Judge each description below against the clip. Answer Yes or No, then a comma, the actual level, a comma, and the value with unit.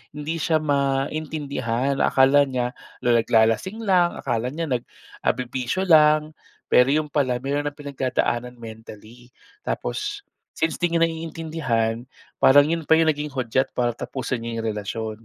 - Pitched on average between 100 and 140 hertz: Yes, low, 135 Hz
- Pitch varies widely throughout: No, average, 4.4 semitones